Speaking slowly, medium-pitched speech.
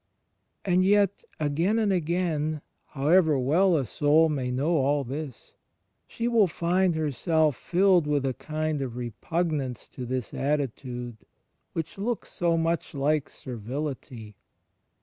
Yes: slow, 130 wpm; medium, 155 Hz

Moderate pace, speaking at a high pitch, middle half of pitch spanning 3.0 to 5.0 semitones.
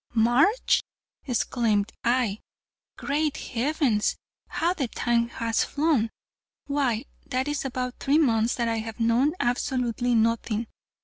No: slow, 120 wpm; high, 245 Hz; average, 3.6 semitones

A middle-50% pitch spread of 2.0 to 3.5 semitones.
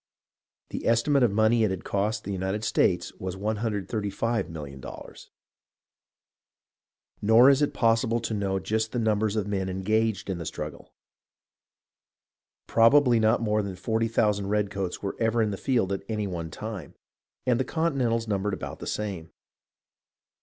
Yes: narrow, 2.6 semitones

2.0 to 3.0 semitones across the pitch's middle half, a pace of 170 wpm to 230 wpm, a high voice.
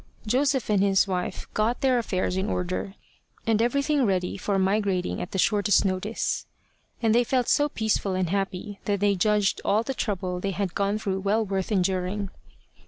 Yes: narrow, 2.5 semitones; average, 175 wpm; high, 200 Hz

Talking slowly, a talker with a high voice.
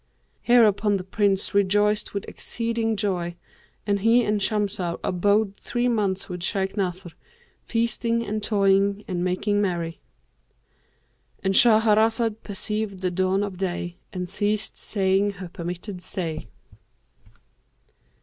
Yes: slow, 120 wpm; high, 200 Hz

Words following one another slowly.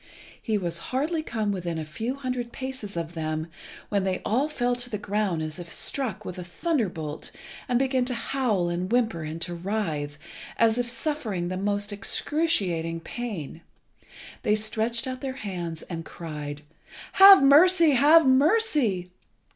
No: average, 155 wpm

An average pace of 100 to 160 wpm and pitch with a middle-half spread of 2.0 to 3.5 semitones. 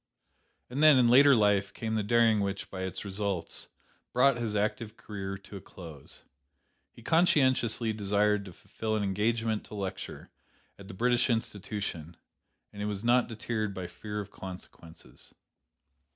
Yes: average, 150 wpm; average, 3.1 semitones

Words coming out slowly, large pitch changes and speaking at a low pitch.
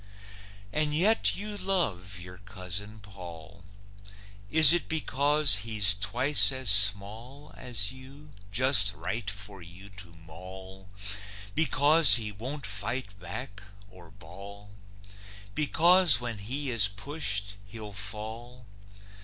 Yes: slow, 110 wpm; wide, 5.7 semitones; low, 105 Hz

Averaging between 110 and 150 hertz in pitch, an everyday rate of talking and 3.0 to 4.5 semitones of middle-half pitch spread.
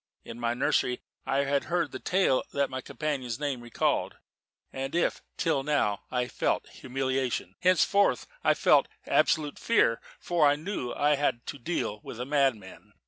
Yes: low, 135 Hz; average, 170 wpm; average, 3.4 semitones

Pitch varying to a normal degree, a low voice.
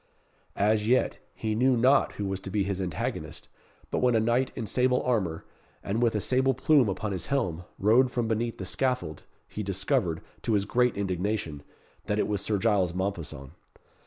Yes: average, 4.2 semitones; low, 105 Hz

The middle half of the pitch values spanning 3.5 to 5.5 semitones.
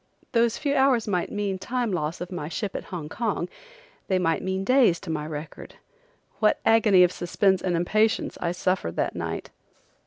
Yes: average, 4.3 semitones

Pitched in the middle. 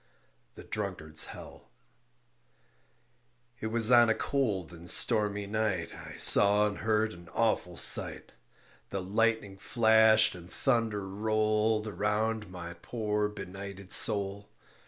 No: low, 105 Hz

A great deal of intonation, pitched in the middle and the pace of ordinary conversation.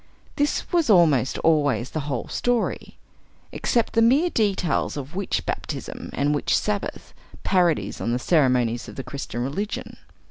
Yes: wide, 8.0 semitones; medium, 155 Hz; average, 150 wpm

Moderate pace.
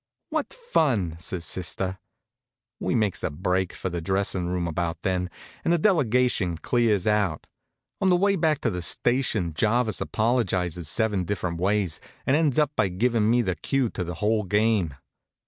Yes: average, 165 wpm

